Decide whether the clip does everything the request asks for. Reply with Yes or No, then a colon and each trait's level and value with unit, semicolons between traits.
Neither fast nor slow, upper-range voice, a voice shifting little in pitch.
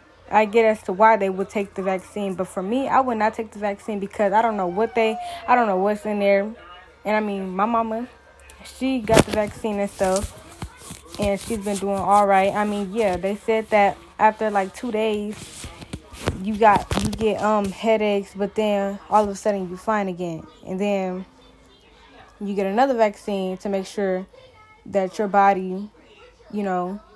Yes: average, 190 wpm; high, 205 Hz; narrow, 2.0 semitones